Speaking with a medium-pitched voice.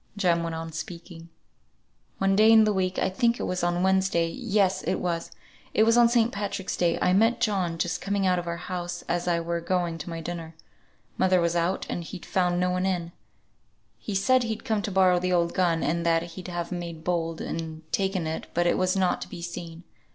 Yes: medium, 180 Hz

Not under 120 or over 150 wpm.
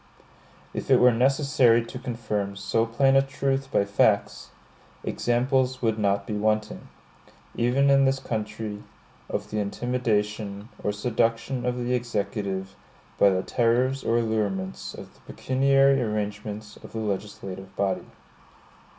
Yes: slow, 135 wpm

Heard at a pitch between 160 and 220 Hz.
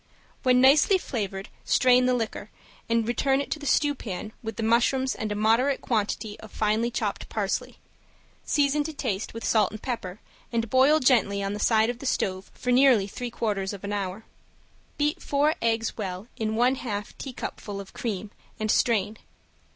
No: high, 230 Hz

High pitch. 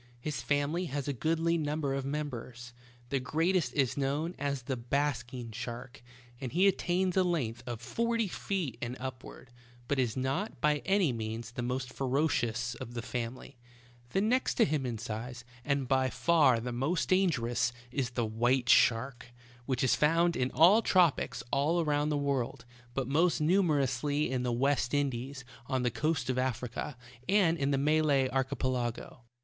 No: low, 135 Hz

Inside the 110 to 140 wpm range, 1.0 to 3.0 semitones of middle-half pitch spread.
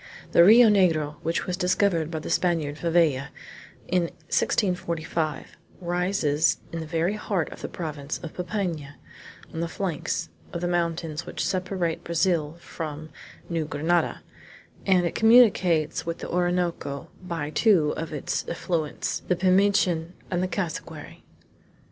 Yes: slow, 135 wpm; narrow, 2.5 semitones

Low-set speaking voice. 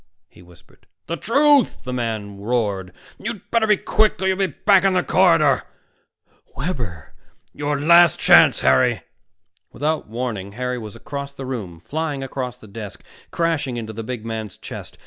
Yes: low, 130 Hz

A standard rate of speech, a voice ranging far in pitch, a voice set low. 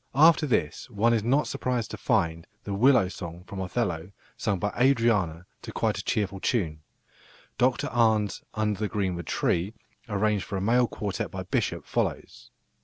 No: average, 165 wpm; average, 4.2 semitones; low, 105 Hz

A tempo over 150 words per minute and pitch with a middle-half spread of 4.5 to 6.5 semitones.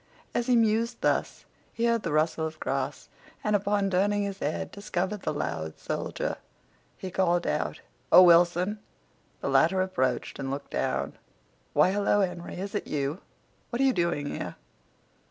Yes: average, 160 wpm; average, 4.9 semitones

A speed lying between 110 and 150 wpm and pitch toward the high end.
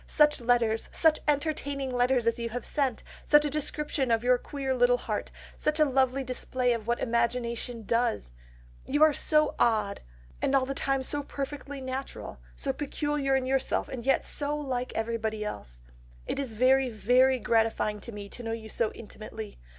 No: average, 180 wpm; very high, 250 Hz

